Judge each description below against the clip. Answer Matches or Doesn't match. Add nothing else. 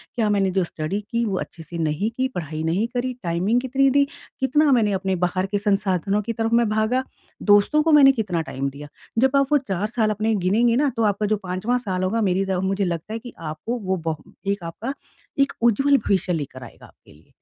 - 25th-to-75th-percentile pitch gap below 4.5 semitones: Doesn't match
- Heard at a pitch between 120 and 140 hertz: Doesn't match